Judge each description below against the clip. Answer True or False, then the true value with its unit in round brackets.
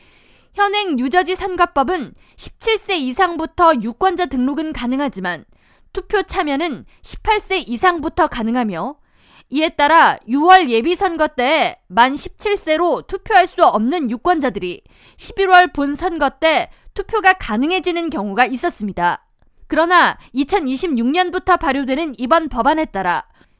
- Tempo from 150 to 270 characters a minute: True (255 characters per minute)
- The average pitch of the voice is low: False (325 Hz)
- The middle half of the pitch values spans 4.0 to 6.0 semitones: True (5.6 semitones)